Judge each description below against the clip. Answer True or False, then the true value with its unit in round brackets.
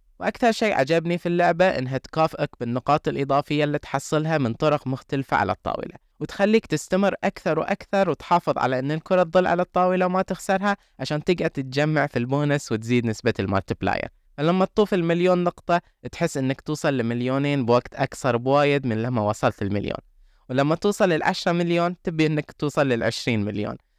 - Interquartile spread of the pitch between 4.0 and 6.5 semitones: True (5.5 semitones)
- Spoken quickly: True (155 wpm)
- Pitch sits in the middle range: True (150 Hz)